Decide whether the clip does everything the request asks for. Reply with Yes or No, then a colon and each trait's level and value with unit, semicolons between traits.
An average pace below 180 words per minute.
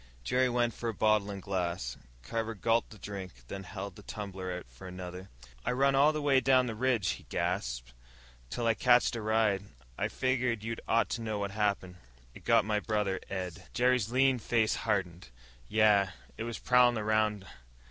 No: average, 185 wpm